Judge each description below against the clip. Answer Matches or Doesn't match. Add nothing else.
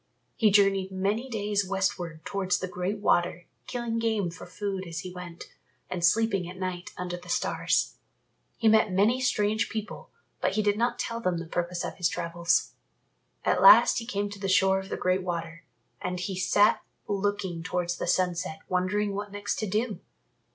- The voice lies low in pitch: Doesn't match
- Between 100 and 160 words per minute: Doesn't match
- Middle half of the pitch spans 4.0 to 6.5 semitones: Doesn't match